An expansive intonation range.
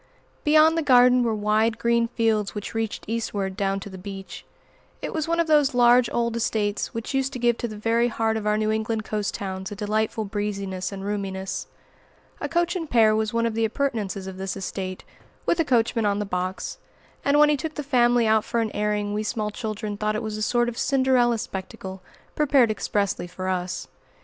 No: average, 2.9 semitones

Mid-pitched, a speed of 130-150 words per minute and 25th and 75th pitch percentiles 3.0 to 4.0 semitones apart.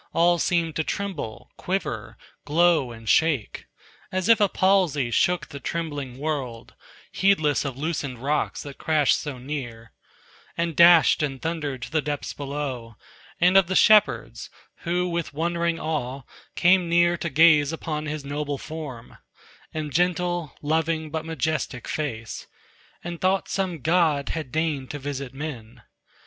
Yes: medium, 155 Hz; average, 145 wpm; average, 3.5 semitones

